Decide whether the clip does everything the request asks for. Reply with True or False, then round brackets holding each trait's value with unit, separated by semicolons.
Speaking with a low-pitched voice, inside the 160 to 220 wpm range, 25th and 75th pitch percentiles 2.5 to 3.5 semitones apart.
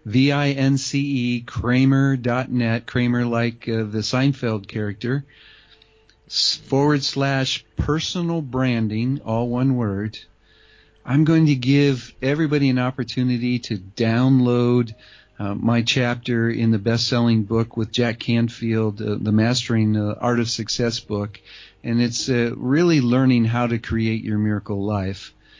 False (120 Hz; 140 wpm; 2.8 semitones)